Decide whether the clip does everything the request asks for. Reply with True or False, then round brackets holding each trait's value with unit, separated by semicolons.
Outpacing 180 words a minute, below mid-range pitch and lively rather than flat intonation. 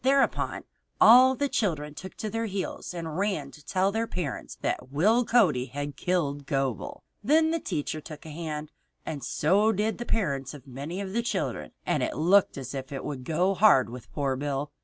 False (195 wpm; 160 Hz; 6.9 semitones)